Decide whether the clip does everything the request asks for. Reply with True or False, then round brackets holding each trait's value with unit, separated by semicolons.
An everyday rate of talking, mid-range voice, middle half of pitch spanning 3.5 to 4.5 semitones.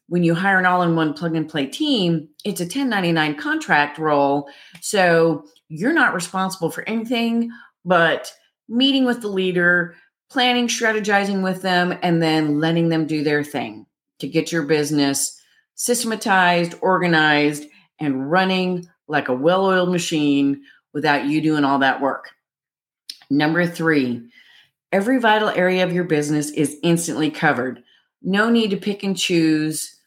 True (150 wpm; 170 Hz; 4.2 semitones)